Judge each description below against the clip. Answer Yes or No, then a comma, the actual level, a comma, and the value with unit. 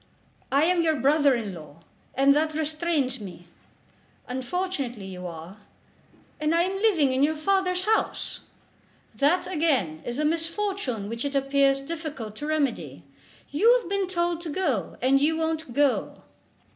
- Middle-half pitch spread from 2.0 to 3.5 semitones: No, average, 4.9 semitones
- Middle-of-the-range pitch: No, very high, 295 Hz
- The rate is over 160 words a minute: No, average, 145 wpm